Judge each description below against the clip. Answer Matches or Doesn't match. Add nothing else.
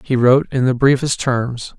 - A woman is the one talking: Doesn't match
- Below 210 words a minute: Matches